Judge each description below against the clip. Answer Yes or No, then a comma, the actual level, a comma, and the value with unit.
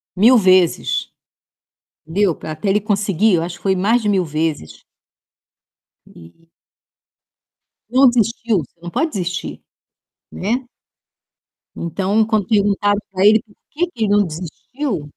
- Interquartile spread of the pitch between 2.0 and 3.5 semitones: No, average, 4.0 semitones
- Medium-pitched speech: No, high, 200 Hz